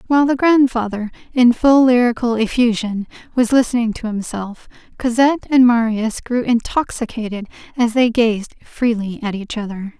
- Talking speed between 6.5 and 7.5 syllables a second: No, 4.9 syllables/s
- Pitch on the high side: Yes, high, 235 Hz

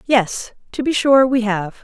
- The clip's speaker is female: Yes, female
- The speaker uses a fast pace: No, average, 195 wpm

